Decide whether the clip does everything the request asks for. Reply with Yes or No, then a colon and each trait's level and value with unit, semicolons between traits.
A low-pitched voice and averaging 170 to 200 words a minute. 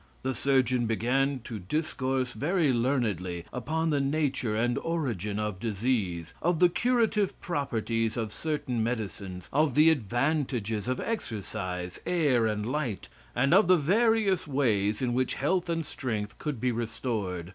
No: low, 125 Hz; average, 145 wpm